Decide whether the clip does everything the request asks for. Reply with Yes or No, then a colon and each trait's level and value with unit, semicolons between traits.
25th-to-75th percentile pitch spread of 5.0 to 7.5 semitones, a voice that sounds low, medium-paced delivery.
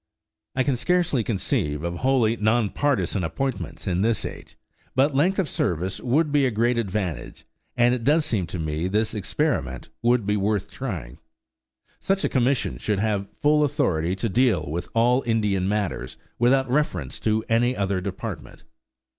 Yes: wide, 5.6 semitones; low, 110 Hz; average, 165 wpm